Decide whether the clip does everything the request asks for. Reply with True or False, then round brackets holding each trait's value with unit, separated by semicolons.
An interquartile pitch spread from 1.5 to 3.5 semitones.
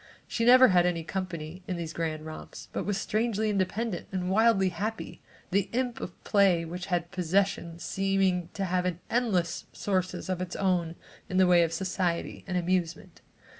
True (2.4 semitones)